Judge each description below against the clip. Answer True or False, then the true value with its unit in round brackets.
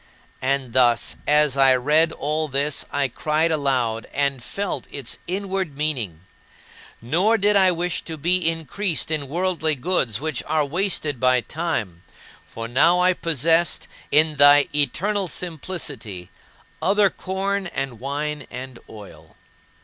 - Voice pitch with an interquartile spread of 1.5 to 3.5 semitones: False (5.0 semitones)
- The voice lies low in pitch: False (150 Hz)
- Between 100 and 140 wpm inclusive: True (135 wpm)